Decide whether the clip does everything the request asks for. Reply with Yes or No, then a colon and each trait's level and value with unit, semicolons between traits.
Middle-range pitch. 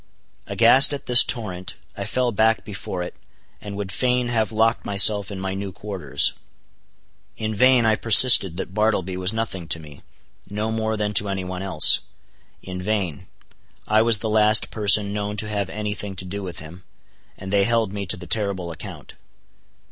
No: low, 105 Hz